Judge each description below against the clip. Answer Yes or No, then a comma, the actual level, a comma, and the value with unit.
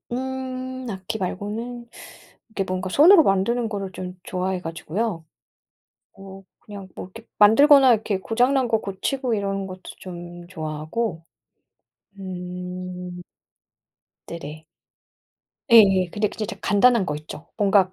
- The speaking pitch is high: Yes, high, 195 Hz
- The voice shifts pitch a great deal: No, average, 4.3 semitones